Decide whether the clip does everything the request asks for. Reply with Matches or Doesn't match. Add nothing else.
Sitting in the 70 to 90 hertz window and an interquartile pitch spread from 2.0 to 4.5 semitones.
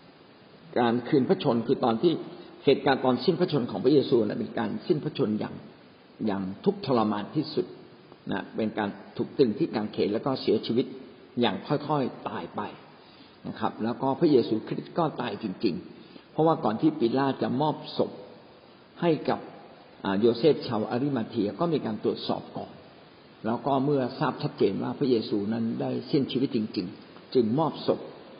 Doesn't match